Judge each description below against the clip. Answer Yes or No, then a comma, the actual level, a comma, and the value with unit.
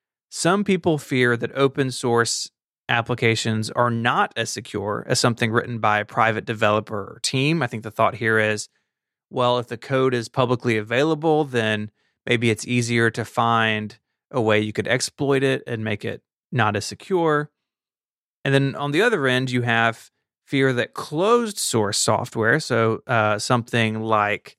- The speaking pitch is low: Yes, low, 120 Hz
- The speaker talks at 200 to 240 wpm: No, average, 165 wpm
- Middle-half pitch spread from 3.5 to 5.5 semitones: No, average, 3.1 semitones